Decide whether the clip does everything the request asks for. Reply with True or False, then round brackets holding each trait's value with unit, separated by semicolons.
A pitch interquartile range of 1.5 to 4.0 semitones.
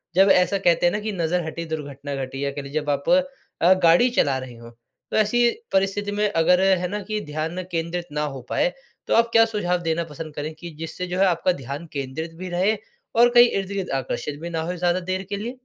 False (4.4 semitones)